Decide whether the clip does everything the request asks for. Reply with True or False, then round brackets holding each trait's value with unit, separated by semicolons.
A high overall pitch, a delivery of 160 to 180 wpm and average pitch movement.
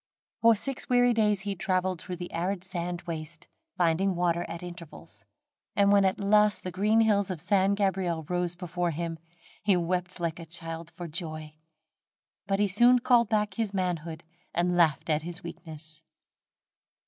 False (180 Hz; 165 wpm; 3.0 semitones)